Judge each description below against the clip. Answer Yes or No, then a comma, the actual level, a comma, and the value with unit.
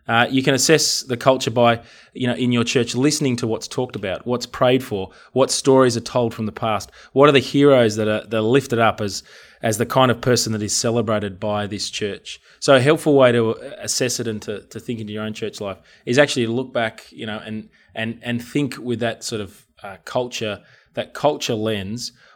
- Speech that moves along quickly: Yes, fast, 230 wpm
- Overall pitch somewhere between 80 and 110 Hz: No, low, 120 Hz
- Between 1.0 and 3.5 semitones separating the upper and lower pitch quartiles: Yes, average, 3.0 semitones